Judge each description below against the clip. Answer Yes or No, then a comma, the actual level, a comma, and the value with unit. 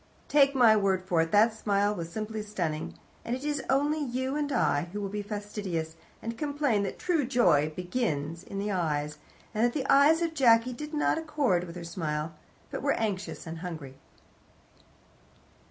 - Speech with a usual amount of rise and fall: No, wide, 7.4 semitones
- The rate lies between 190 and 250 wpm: No, average, 180 wpm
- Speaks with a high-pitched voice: Yes, high, 210 Hz